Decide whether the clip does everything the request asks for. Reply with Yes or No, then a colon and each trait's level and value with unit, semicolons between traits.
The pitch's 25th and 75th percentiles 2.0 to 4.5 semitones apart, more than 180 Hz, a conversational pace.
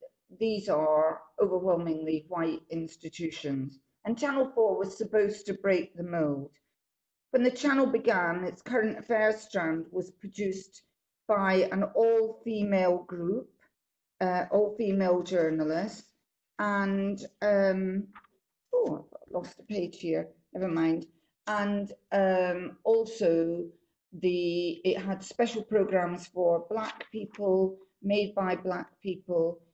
No: average, 3.5 semitones; high, 190 Hz; slow, 115 wpm